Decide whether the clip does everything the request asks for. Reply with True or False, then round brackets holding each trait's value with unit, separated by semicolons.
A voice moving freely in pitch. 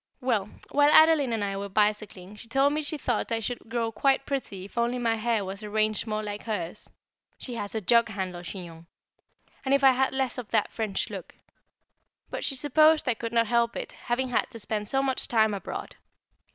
False (4.0 semitones)